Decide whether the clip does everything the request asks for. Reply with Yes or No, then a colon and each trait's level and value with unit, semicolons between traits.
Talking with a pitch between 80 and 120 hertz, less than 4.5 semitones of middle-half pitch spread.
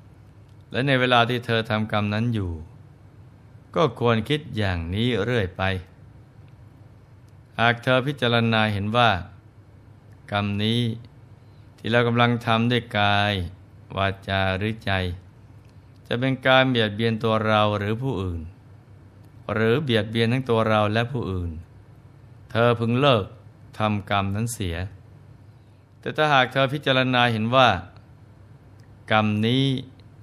Yes: low, 110 Hz; narrow, 2.5 semitones